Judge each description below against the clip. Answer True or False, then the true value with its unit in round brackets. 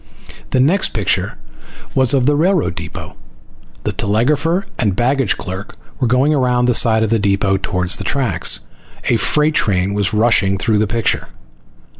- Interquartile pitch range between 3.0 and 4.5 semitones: False (5.3 semitones)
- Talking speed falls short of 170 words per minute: True (160 wpm)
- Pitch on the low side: True (115 Hz)